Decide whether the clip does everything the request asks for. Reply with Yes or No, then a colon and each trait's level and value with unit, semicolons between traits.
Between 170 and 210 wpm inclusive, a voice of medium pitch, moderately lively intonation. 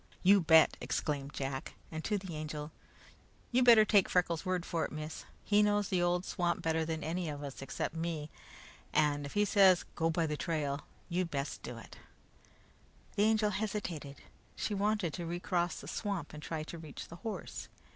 Yes: average, 185 wpm; medium, 170 Hz; average, 4.2 semitones